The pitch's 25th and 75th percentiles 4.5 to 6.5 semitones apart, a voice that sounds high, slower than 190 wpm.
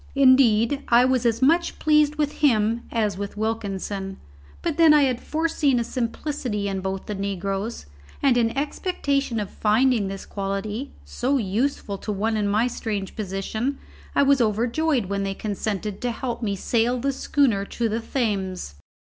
Yes: average, 5.0 semitones; high, 225 Hz; average, 165 wpm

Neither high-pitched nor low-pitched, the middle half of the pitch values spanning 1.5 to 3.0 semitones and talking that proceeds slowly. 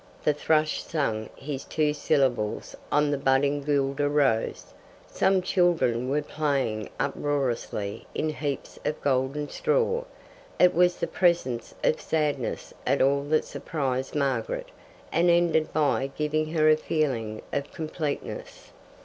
Yes: medium, 145 Hz; average, 2.7 semitones; slow, 130 wpm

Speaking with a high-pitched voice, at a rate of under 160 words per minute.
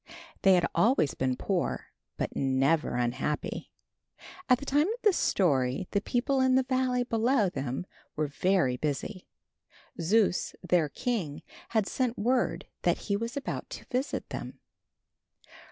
Yes: high, 200 Hz; average, 140 wpm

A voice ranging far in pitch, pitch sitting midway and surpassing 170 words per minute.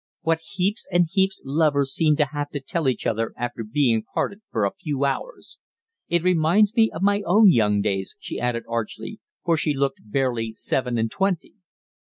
Yes: wide, 7.0 semitones; medium, 145 Hz; average, 190 wpm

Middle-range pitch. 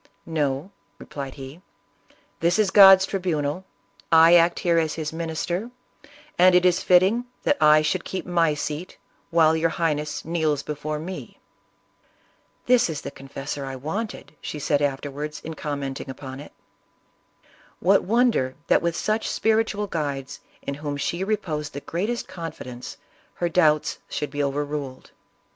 Yes: medium, 160 Hz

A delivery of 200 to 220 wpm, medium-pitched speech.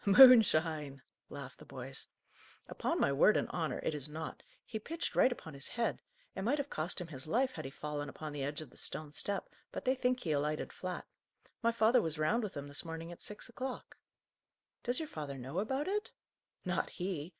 Yes: fast, 205 wpm; medium, 170 Hz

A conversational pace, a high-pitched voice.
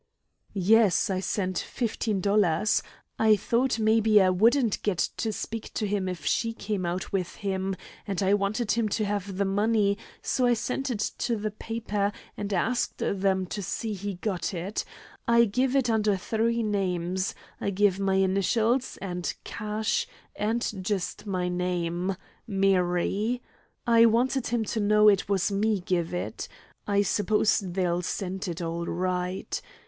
Yes: average, 155 wpm; high, 200 Hz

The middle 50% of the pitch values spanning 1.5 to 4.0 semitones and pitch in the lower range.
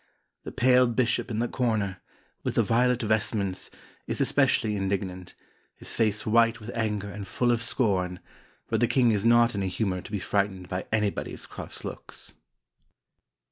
Yes: average, 3.2 semitones; low, 110 Hz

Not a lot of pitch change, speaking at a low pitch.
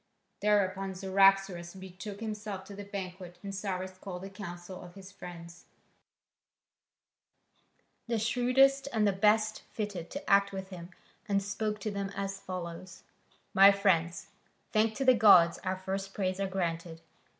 No: narrow, 2.0 semitones; high, 195 Hz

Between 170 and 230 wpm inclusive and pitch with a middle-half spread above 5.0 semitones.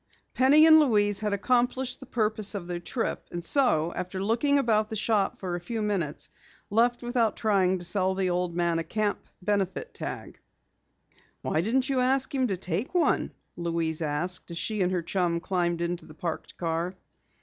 Yes: average, 180 wpm; wide, 5.4 semitones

